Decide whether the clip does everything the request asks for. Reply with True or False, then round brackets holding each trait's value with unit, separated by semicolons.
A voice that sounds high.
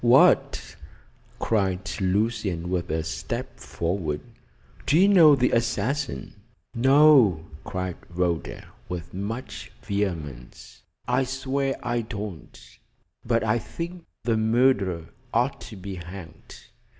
False (105 Hz)